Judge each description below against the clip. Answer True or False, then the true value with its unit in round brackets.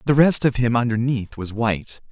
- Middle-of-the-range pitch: False (120 Hz)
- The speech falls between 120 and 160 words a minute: False (200 wpm)